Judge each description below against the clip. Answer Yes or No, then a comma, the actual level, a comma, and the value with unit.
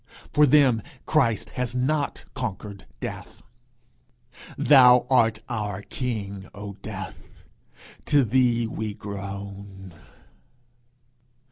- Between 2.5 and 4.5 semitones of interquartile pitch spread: Yes, average, 4.0 semitones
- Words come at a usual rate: No, slow, 90 wpm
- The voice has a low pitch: Yes, low, 110 Hz